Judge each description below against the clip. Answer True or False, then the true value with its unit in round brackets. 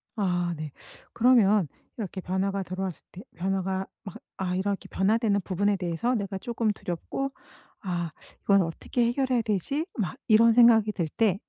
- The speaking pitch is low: False (200 Hz)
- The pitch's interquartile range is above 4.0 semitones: False (3.5 semitones)